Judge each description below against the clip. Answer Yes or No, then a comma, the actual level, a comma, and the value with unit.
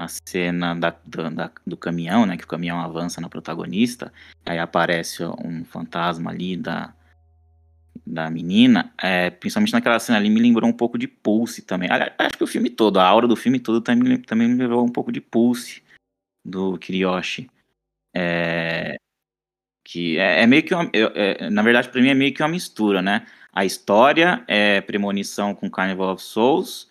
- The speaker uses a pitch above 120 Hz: No, low, 100 Hz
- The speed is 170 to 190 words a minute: Yes, average, 180 wpm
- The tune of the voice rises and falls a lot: Yes, wide, 6.8 semitones